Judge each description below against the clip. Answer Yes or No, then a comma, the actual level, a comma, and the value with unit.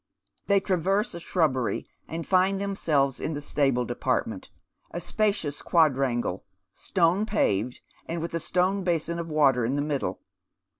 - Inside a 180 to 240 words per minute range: No, average, 140 wpm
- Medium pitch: Yes, medium, 165 Hz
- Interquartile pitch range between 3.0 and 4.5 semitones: No, average, 5.0 semitones